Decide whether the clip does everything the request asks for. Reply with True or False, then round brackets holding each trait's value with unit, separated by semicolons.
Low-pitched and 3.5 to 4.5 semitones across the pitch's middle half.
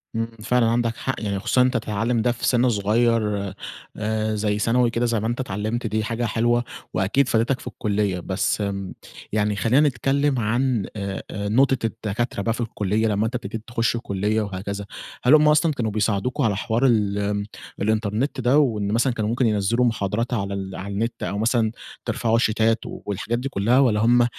False (110 Hz; 2.7 semitones)